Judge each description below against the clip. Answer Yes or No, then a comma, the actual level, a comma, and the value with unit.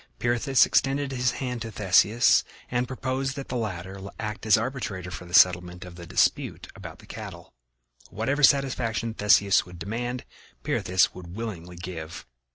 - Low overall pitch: Yes, low, 110 Hz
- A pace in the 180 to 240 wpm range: No, average, 155 wpm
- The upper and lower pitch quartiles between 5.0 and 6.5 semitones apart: Yes, wide, 5.6 semitones